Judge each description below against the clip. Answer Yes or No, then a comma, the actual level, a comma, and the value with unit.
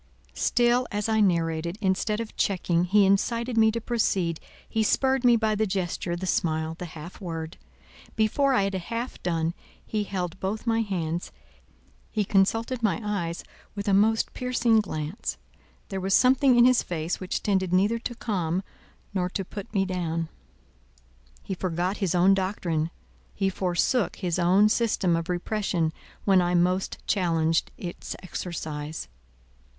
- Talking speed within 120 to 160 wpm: Yes, average, 155 wpm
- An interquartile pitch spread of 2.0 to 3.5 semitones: No, average, 4.0 semitones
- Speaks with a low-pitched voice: No, high, 190 Hz